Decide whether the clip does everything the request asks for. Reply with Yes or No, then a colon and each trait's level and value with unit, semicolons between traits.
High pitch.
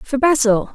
Yes: very high, 260 Hz